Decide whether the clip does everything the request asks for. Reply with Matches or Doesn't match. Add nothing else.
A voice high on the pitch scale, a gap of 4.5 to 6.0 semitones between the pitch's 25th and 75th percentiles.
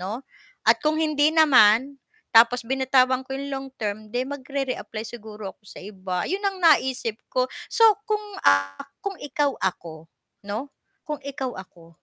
Matches